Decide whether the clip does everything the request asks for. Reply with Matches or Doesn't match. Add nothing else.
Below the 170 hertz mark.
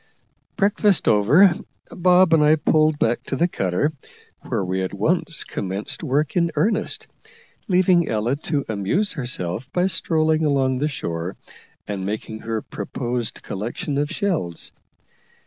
Matches